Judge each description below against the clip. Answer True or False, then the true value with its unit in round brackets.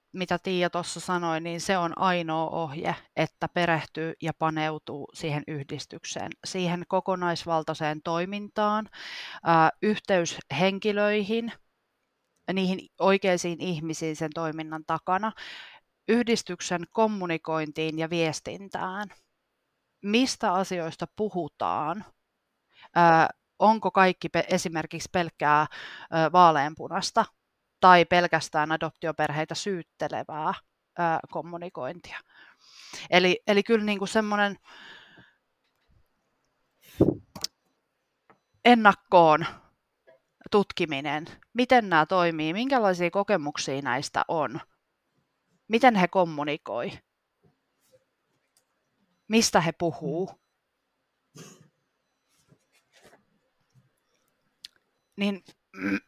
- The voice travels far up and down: False (3.4 semitones)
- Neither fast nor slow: False (70 wpm)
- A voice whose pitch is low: False (175 Hz)